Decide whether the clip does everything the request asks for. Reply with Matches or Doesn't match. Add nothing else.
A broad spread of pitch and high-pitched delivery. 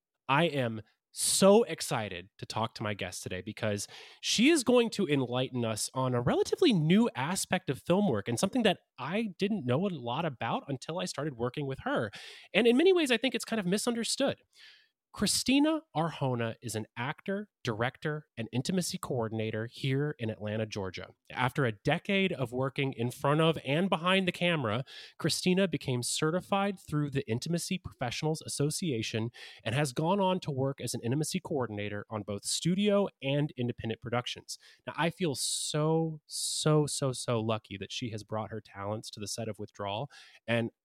Doesn't match